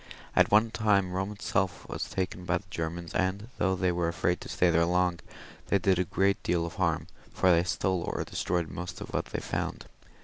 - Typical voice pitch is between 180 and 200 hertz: No, very low, 90 Hz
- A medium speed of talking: No, fast, 210 wpm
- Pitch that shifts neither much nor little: No, narrow, 1.8 semitones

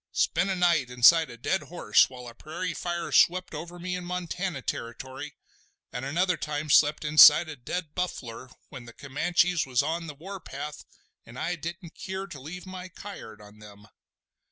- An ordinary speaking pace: Yes, average, 175 wpm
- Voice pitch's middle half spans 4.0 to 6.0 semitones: Yes, average, 5.2 semitones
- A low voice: No, medium, 160 Hz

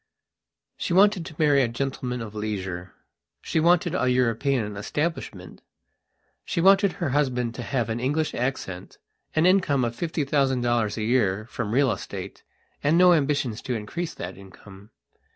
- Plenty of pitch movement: Yes, wide, 6.3 semitones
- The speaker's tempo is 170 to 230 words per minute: No, average, 155 wpm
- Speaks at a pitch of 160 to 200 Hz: No, low, 130 Hz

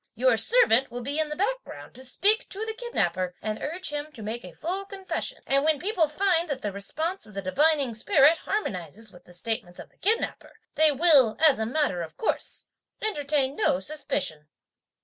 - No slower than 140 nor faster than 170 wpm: No, average, 190 wpm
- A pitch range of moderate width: No, wide, 8.2 semitones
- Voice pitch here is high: Yes, very high, 290 Hz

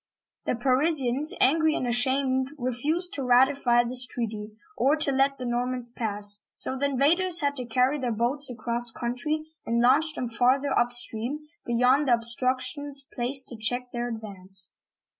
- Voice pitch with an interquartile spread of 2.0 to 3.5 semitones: Yes, average, 2.7 semitones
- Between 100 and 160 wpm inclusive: Yes, average, 155 wpm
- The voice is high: Yes, very high, 255 Hz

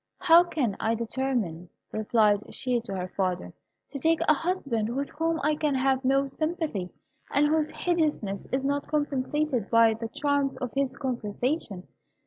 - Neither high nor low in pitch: No, very high, 265 Hz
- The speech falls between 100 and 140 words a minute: No, average, 160 wpm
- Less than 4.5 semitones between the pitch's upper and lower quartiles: No, average, 5.2 semitones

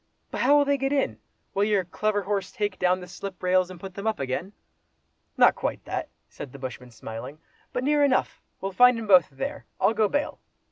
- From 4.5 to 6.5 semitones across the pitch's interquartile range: Yes, average, 5.1 semitones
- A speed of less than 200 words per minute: No, fast, 205 wpm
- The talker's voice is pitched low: No, high, 195 Hz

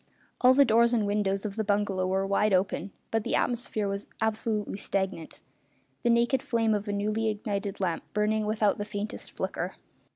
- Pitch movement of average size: No, narrow, 2.0 semitones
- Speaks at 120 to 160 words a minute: No, average, 175 wpm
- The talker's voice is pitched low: No, high, 210 Hz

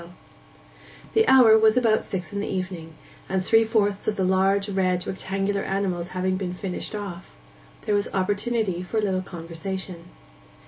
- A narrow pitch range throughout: Yes, narrow, 2.0 semitones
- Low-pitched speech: No, high, 195 Hz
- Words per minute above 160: No, average, 155 wpm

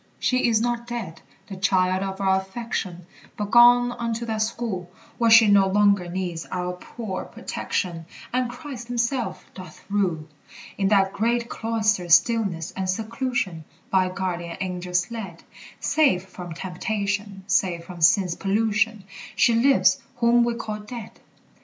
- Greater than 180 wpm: No, average, 140 wpm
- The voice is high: Yes, high, 200 Hz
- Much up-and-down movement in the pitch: No, average, 4.1 semitones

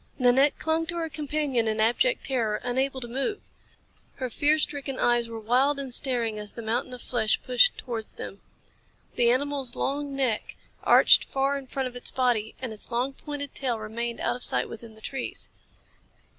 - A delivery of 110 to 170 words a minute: No, average, 185 wpm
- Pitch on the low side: No, very high, 255 Hz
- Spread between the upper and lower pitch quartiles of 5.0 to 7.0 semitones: No, average, 3.0 semitones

